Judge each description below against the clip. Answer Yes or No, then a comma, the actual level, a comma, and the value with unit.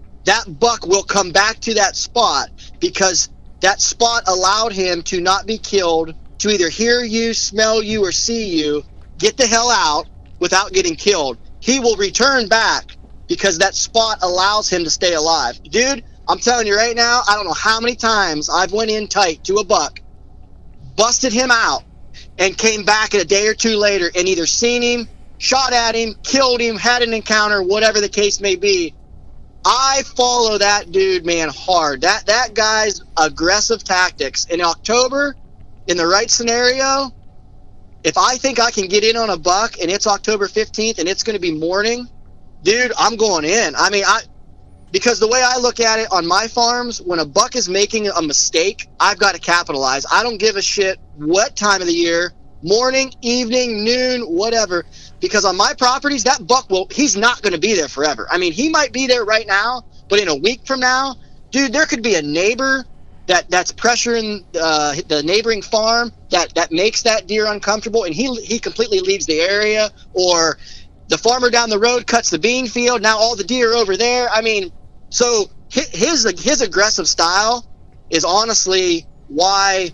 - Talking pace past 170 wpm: Yes, average, 190 wpm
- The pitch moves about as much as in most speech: Yes, average, 4.0 semitones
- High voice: Yes, high, 220 Hz